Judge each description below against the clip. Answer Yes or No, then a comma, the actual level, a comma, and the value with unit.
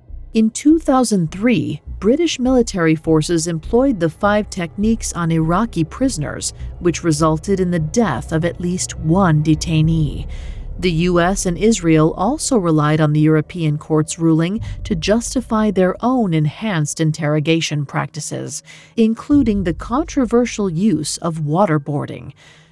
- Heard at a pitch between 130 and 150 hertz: No, medium, 170 Hz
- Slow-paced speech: Yes, slow, 120 wpm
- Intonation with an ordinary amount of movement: No, wide, 5.7 semitones